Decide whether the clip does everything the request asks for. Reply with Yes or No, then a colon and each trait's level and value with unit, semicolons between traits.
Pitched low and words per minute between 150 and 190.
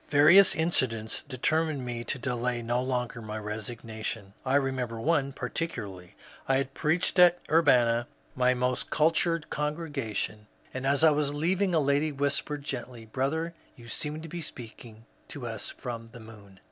Yes: low, 130 Hz; average, 160 wpm